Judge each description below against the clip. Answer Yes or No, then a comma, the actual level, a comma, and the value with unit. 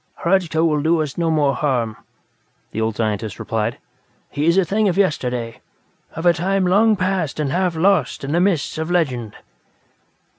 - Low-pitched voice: No, medium, 160 Hz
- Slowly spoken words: No, average, 175 wpm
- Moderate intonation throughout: No, wide, 5.8 semitones